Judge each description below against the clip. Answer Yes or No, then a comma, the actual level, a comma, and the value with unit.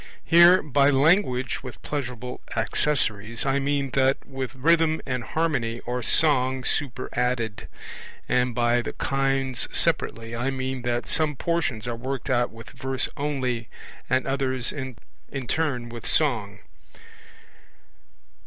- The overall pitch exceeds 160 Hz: No, low, 130 Hz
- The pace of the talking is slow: Yes, slow, 125 wpm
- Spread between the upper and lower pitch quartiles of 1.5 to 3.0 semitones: Yes, narrow, 2.6 semitones